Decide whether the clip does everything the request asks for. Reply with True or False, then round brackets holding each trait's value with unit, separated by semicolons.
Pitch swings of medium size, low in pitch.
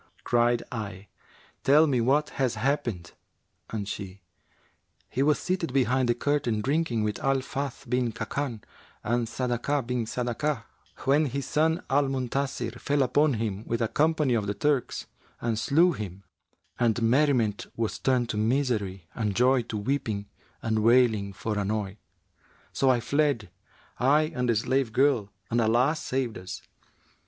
True (4.0 semitones; 120 Hz)